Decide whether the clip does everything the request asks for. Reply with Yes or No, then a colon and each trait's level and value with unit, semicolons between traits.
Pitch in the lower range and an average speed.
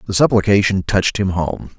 Yes: low, 100 Hz; average, 170 wpm